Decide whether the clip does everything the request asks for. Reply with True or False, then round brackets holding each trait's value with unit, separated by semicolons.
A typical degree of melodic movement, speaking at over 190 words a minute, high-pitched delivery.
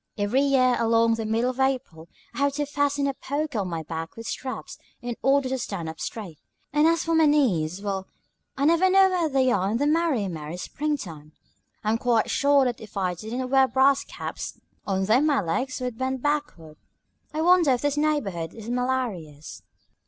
False (6.3 semitones; 200 wpm; 255 Hz)